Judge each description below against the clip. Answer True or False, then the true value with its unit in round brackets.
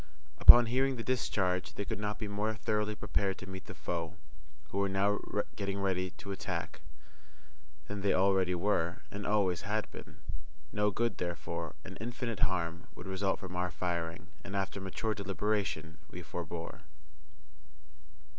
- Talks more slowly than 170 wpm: True (155 wpm)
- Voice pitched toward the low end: True (95 Hz)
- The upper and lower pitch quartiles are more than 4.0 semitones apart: False (2.7 semitones)